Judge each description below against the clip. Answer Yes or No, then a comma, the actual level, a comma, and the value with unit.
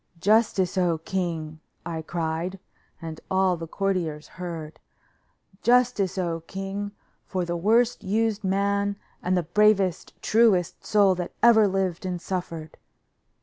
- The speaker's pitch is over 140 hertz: Yes, medium, 185 Hz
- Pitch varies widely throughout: No, average, 3.1 semitones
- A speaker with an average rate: No, slow, 125 wpm